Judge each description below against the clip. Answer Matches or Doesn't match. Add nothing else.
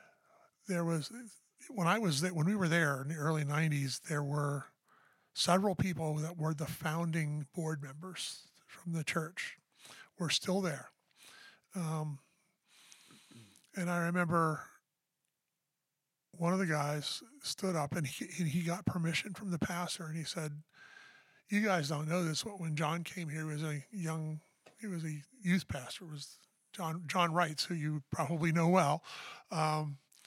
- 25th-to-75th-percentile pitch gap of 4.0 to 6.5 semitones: Doesn't match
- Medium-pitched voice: Matches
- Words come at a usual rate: Matches